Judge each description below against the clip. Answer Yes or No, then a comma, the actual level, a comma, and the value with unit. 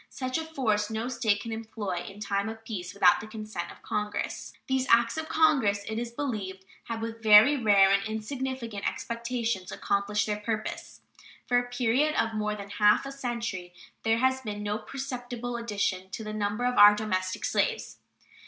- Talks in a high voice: Yes, high, 220 Hz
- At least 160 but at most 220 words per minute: Yes, average, 180 wpm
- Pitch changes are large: No, average, 2.9 semitones